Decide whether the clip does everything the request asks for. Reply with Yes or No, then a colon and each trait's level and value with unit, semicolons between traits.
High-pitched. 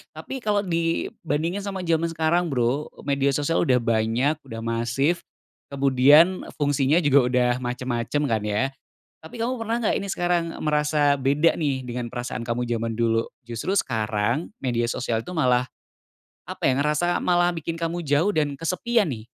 No: medium, 145 Hz